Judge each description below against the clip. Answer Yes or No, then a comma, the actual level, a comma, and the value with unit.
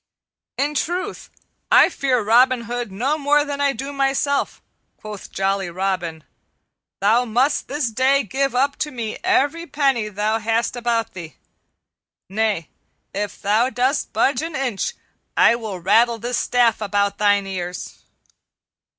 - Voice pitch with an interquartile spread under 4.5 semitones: No, average, 5.0 semitones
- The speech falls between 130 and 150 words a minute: Yes, average, 140 wpm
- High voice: Yes, high, 235 Hz